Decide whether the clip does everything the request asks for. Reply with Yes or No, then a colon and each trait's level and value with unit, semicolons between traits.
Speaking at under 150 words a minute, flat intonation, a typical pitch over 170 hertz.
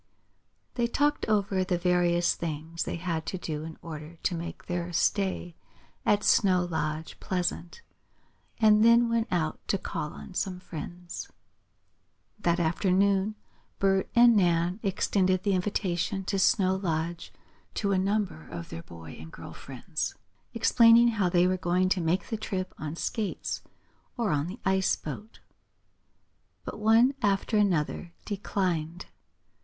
No: average, 140 wpm; average, 3.2 semitones; medium, 185 Hz